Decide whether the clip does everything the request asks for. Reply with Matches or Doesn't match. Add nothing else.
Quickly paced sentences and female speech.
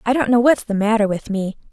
Matches